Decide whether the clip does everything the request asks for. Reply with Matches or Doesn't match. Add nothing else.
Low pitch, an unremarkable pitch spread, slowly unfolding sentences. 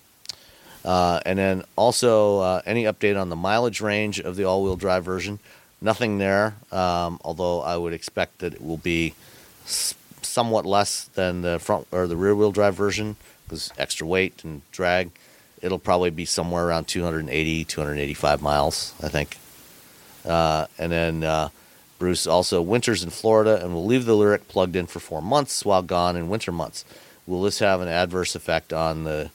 Doesn't match